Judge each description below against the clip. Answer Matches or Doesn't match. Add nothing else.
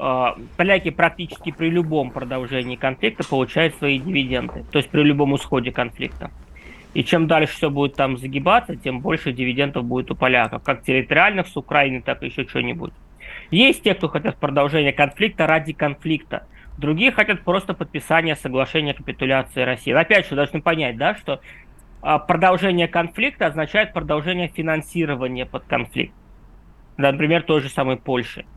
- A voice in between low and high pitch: Matches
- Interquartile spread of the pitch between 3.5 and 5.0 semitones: Matches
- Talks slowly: Doesn't match